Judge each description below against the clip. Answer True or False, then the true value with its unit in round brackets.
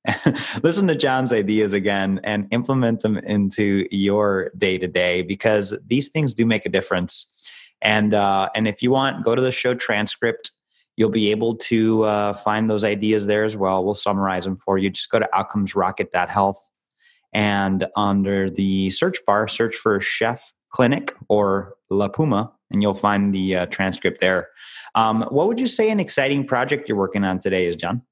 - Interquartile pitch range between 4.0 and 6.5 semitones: False (2.7 semitones)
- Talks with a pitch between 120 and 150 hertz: False (105 Hz)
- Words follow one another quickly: False (175 wpm)